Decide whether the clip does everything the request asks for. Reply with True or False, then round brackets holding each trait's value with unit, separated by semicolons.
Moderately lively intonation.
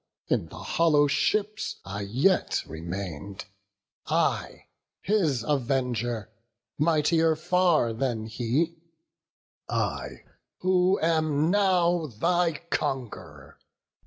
False (7.1 semitones)